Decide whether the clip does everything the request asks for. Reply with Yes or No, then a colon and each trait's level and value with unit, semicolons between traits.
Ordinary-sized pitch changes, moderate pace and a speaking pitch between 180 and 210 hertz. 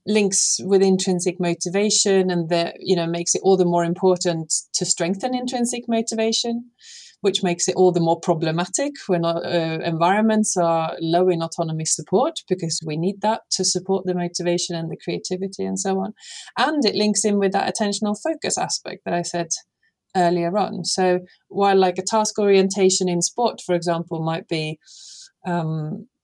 Yes: average, 3.3 semitones; average, 170 wpm; medium, 185 Hz